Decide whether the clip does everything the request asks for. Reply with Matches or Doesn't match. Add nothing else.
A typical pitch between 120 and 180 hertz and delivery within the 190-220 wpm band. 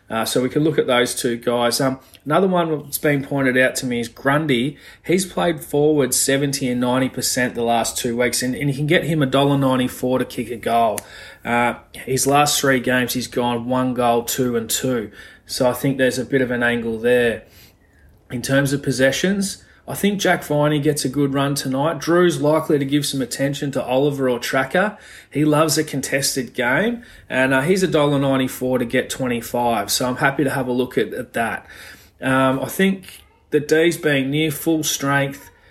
Matches